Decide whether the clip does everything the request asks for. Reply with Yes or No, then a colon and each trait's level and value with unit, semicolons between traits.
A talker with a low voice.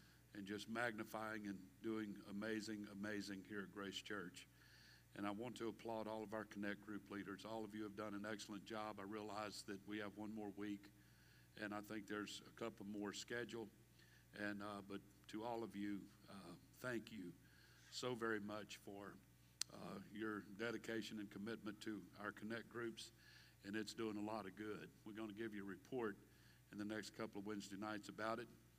Yes: low, 105 Hz